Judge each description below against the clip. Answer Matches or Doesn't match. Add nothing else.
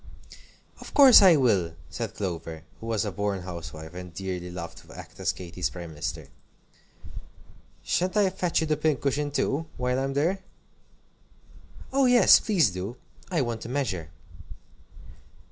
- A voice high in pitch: Doesn't match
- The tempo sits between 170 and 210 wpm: Doesn't match